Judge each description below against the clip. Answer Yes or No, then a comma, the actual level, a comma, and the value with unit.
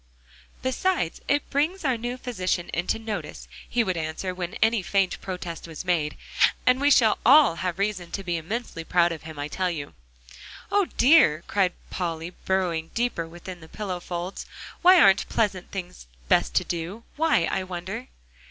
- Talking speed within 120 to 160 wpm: No, average, 170 wpm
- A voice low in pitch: No, medium, 185 Hz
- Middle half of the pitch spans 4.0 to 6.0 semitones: Yes, wide, 5.4 semitones